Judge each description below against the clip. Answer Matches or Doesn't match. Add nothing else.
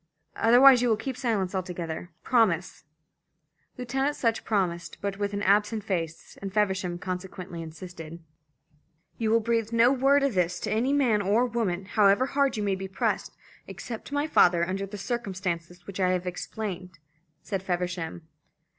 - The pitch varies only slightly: Doesn't match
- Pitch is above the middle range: Matches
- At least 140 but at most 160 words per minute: Matches